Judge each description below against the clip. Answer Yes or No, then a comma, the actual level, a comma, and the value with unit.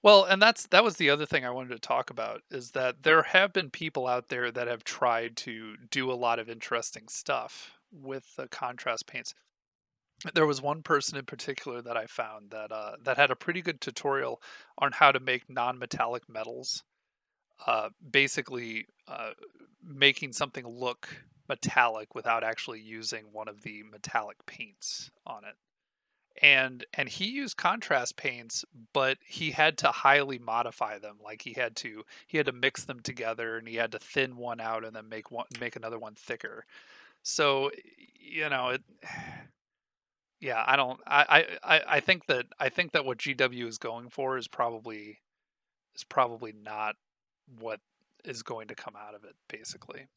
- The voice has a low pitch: Yes, low, 130 Hz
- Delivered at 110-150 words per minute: No, average, 175 wpm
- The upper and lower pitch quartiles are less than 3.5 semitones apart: No, average, 4.0 semitones